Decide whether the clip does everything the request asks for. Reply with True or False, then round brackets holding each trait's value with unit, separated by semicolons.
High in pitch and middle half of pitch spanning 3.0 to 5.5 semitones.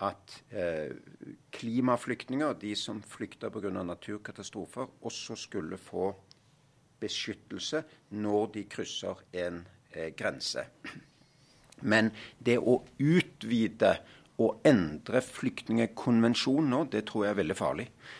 False (115 Hz; 3.3 semitones)